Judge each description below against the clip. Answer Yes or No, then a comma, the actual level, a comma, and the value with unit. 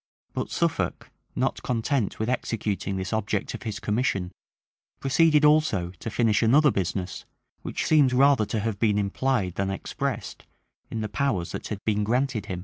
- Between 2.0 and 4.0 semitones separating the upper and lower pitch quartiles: No, average, 4.8 semitones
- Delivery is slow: No, average, 165 wpm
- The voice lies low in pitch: Yes, low, 110 Hz